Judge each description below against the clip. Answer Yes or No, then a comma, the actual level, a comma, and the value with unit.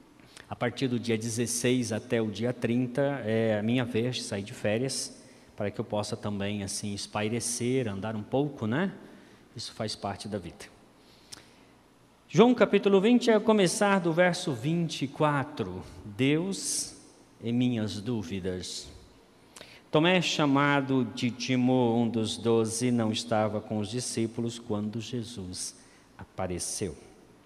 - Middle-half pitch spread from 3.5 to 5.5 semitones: Yes, average, 4.2 semitones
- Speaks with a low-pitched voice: Yes, low, 120 Hz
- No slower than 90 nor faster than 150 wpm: Yes, average, 135 wpm